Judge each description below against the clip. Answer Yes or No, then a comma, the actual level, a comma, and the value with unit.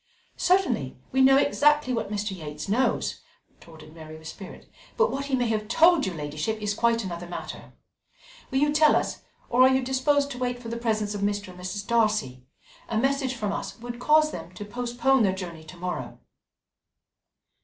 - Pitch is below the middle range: No, high, 225 Hz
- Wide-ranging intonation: Yes, wide, 6.2 semitones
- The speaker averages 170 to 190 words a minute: Yes, average, 185 wpm